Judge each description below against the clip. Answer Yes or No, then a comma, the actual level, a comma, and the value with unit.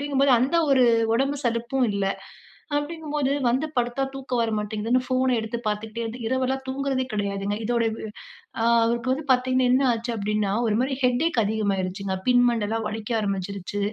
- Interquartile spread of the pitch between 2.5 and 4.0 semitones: Yes, average, 3.6 semitones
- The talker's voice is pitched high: Yes, high, 235 Hz